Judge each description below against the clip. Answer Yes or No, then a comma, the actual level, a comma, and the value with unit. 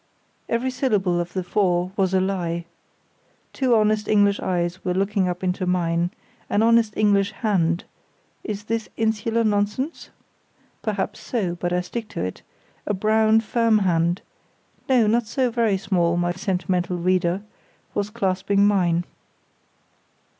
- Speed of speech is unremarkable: No, slow, 125 wpm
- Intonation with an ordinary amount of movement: Yes, average, 3.4 semitones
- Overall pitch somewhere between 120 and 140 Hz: No, high, 195 Hz